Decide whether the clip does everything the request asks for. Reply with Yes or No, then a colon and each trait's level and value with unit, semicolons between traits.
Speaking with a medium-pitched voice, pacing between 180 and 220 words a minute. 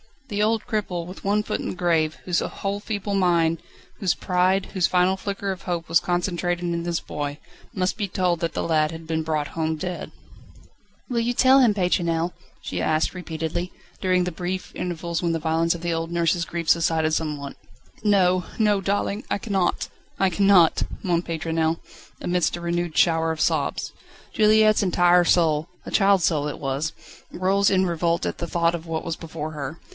Yes: medium, 175 Hz; average, 185 wpm